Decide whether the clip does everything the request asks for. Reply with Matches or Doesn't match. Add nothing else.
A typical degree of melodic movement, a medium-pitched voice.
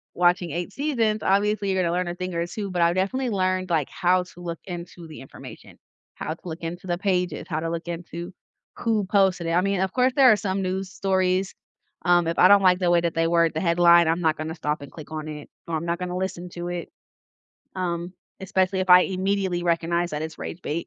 Doesn't match